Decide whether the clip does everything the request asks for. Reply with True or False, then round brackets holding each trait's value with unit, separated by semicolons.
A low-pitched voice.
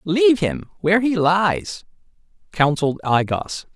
False (170 Hz)